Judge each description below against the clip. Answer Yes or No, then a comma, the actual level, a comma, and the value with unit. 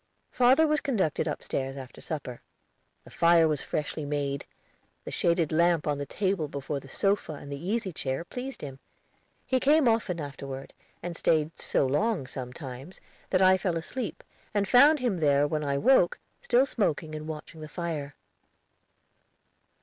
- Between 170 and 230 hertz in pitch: No, medium, 160 Hz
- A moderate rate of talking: Yes, average, 155 wpm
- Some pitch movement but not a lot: No, wide, 6.0 semitones